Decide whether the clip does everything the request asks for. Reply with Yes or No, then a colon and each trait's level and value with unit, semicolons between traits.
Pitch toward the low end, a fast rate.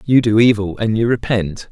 Yes: low, 110 Hz; fast, 210 wpm